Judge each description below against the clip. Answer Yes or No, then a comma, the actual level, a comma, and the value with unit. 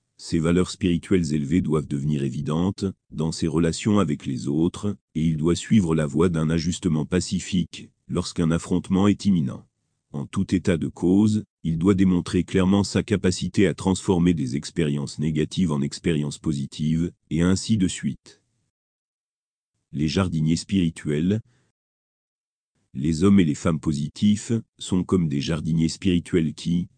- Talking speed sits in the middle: No, slow, 140 wpm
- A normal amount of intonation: Yes, average, 3.6 semitones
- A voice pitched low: Yes, very low, 85 Hz